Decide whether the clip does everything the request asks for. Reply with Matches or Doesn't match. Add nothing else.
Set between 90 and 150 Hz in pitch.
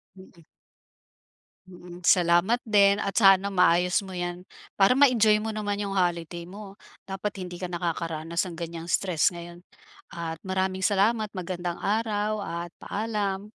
Doesn't match